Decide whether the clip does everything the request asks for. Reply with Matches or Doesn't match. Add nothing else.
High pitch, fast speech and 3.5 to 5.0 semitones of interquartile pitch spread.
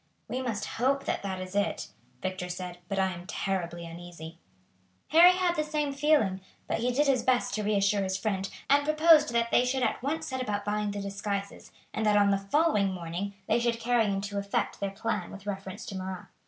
Matches